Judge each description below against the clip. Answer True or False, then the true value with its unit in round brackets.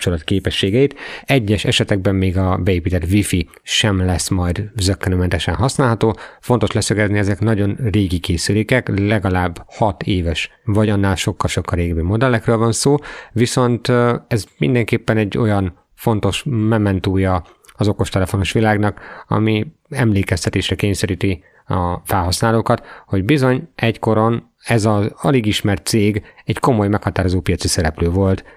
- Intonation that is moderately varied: True (3.1 semitones)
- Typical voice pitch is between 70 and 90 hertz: False (105 Hz)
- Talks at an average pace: True (120 wpm)